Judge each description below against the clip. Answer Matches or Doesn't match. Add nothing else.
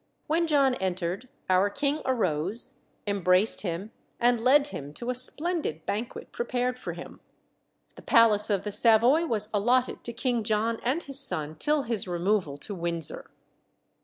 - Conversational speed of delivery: Matches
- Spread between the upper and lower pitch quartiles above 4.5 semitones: Matches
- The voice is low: Doesn't match